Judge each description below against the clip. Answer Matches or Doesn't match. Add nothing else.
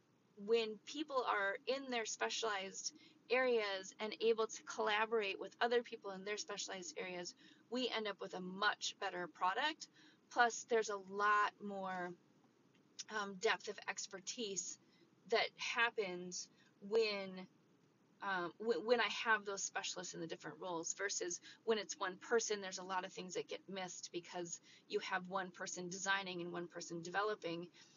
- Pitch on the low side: Doesn't match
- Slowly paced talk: Doesn't match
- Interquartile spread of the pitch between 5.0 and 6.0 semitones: Doesn't match